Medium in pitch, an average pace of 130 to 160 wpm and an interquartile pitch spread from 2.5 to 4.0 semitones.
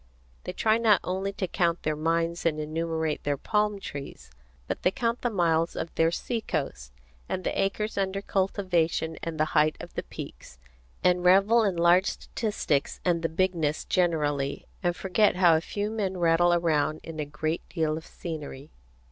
No: medium, 170 Hz; average, 175 wpm; average, 3.5 semitones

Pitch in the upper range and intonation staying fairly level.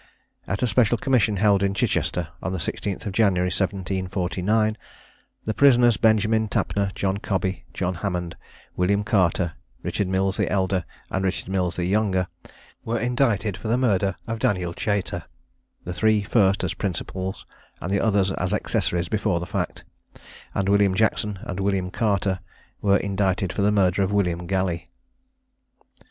No: low, 100 Hz; narrow, 2.2 semitones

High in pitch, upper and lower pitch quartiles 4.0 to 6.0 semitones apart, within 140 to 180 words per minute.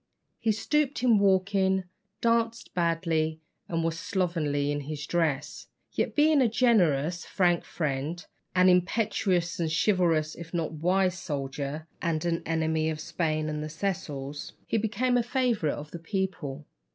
No: medium, 170 Hz; average, 4.3 semitones; average, 145 wpm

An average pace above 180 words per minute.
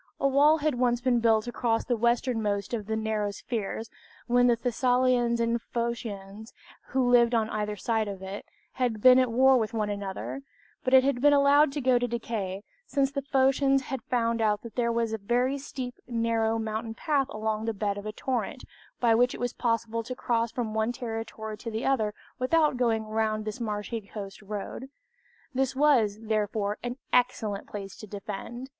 Yes: average, 190 wpm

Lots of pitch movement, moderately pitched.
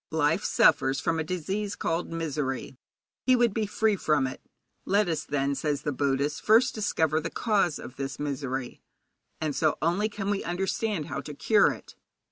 Yes: wide, 6.0 semitones; medium, 160 Hz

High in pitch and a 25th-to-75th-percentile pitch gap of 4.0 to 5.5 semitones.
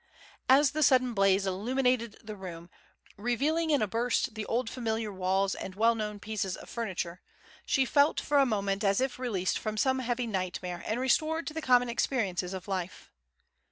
Yes: high, 220 Hz; average, 4.7 semitones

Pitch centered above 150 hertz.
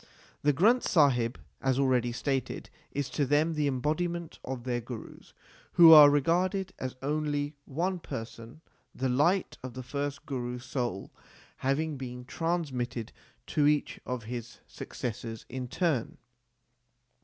No: low, 135 Hz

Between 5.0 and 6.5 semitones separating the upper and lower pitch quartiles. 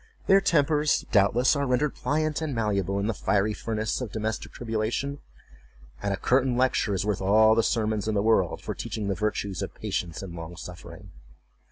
No: average, 4.3 semitones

